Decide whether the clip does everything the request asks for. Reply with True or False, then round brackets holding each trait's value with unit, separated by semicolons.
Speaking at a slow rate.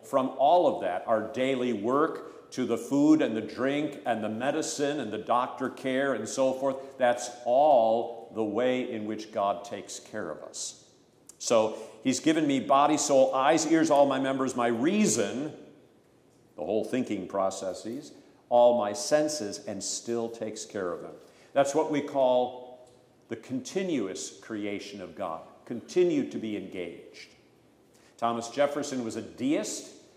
False (155 wpm)